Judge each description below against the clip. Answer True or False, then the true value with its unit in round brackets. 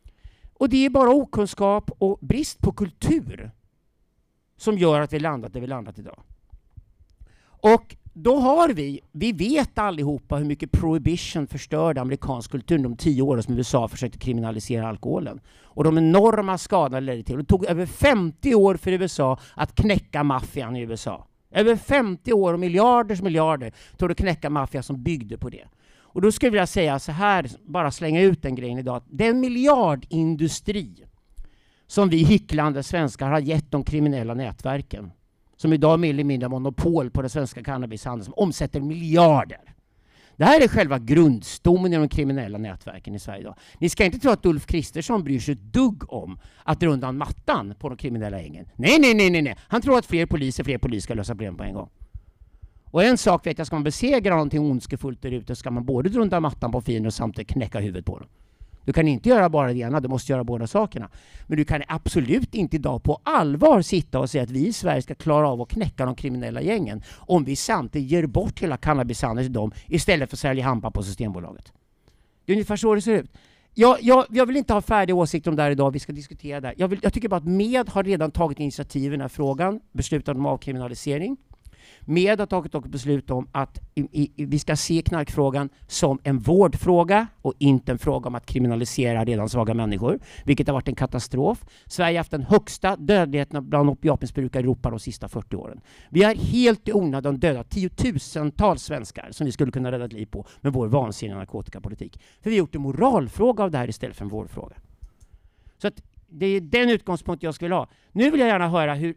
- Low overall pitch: False (145 Hz)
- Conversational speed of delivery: False (205 wpm)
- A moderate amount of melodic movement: False (6.3 semitones)